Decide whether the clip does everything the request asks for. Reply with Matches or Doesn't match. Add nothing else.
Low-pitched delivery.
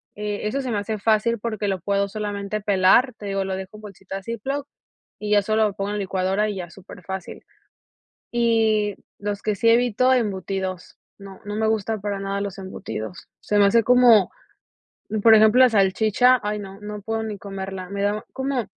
Doesn't match